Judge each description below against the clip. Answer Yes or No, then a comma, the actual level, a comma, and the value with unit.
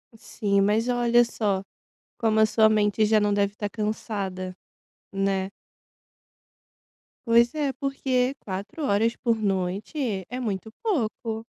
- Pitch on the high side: Yes, high, 215 Hz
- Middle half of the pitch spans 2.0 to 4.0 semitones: Yes, average, 3.0 semitones